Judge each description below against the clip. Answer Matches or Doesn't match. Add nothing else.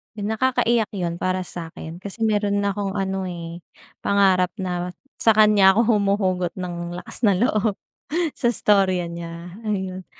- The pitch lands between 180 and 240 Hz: Matches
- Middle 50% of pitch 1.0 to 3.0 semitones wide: Matches